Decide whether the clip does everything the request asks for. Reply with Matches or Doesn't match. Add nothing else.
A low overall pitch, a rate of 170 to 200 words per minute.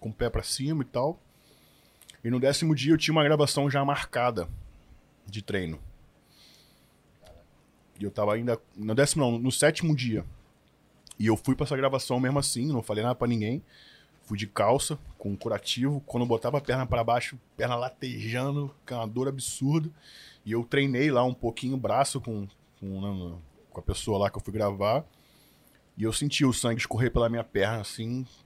Matches